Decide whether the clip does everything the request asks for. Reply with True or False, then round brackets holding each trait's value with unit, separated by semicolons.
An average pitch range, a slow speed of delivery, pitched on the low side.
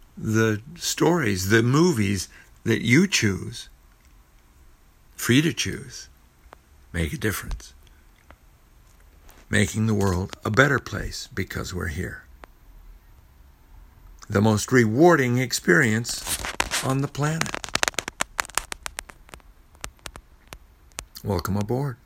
False (7.3 semitones; 85 wpm; 105 Hz)